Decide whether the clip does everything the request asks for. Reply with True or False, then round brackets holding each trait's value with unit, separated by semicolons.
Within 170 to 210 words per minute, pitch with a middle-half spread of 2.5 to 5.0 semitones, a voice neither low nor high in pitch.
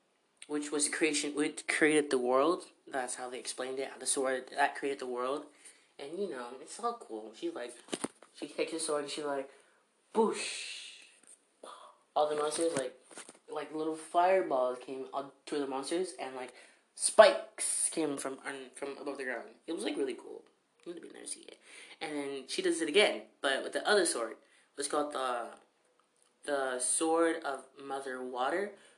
True (180 wpm; 3.3 semitones; 145 Hz)